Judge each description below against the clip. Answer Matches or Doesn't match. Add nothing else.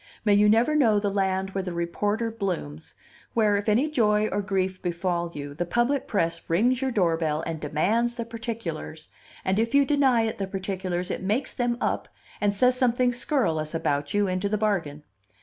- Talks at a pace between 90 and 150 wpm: Doesn't match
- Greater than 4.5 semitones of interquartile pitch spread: Matches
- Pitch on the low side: Doesn't match